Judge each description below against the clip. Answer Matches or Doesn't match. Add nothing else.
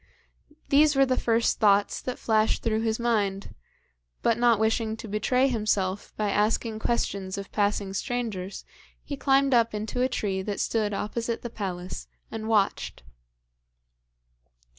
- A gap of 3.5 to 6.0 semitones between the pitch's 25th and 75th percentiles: Doesn't match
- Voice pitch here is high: Matches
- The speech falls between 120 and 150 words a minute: Matches